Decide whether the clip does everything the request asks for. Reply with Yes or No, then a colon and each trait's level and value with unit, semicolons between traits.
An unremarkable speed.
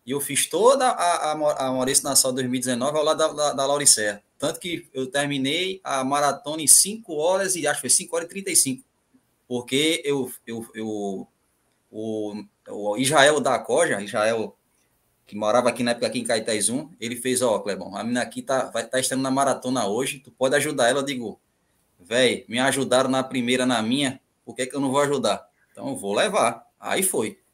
No: fast, 205 wpm